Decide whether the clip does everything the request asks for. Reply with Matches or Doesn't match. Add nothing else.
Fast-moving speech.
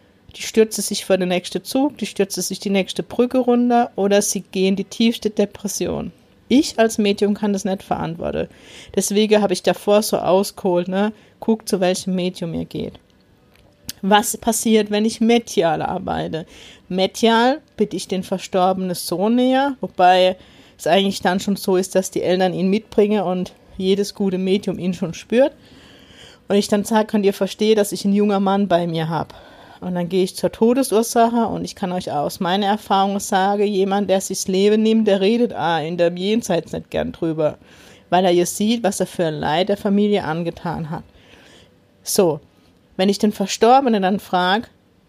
Doesn't match